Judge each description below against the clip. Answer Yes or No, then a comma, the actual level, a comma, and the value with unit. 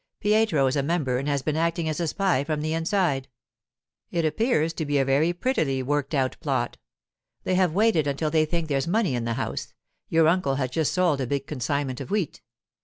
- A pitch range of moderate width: Yes, average, 3.9 semitones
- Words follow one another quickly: Yes, fast, 210 wpm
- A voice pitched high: No, medium, 155 Hz